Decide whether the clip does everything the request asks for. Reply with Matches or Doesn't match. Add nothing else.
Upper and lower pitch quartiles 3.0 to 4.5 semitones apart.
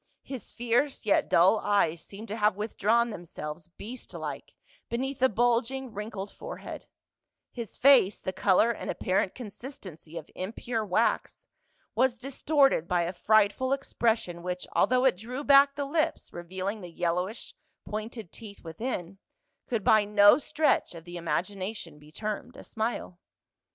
Doesn't match